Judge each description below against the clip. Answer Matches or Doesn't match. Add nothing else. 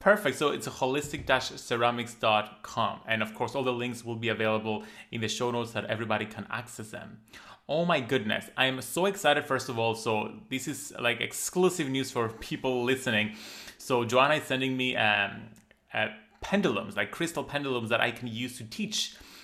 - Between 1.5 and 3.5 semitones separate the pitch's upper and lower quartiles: Matches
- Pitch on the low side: Matches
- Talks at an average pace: Matches